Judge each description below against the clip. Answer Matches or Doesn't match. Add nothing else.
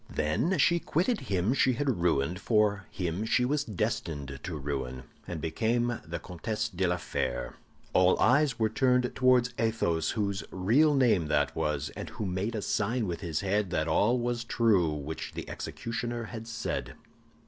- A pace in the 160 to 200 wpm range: Matches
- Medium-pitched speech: Doesn't match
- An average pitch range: Doesn't match